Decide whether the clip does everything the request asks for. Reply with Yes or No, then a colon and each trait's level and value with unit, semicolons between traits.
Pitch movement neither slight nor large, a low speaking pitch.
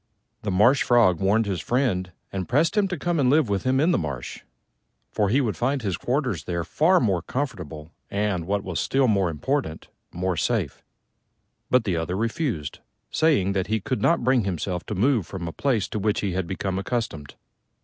No: wide, 6.1 semitones; low, 105 Hz